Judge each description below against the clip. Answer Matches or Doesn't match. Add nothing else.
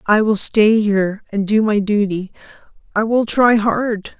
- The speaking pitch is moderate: Doesn't match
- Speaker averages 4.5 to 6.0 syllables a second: Doesn't match